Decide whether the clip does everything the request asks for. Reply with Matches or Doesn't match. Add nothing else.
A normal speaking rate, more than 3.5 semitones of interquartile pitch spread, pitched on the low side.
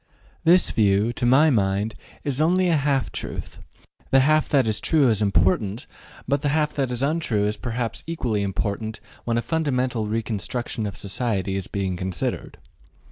Matches